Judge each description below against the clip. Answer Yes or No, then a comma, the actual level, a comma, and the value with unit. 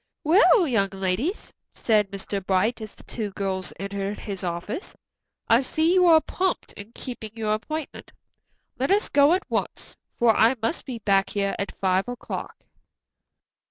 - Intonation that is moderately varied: No, wide, 6.3 semitones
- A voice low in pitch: No, high, 220 Hz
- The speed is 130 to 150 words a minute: No, average, 160 wpm